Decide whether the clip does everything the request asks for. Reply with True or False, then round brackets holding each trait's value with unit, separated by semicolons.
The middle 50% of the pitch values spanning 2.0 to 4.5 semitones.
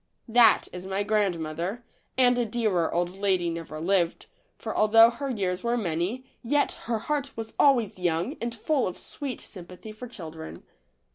False (5.3 semitones)